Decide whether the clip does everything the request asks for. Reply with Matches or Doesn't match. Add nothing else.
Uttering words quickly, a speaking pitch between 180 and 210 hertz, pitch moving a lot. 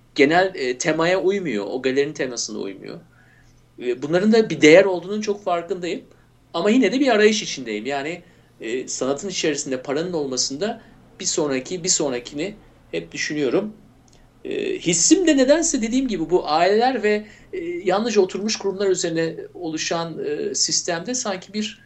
Matches